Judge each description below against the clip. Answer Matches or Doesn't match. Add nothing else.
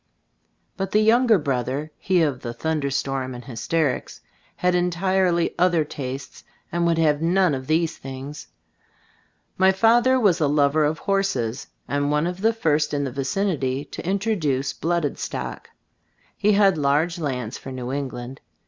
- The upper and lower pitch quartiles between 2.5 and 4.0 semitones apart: Doesn't match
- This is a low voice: Doesn't match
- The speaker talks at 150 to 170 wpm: Matches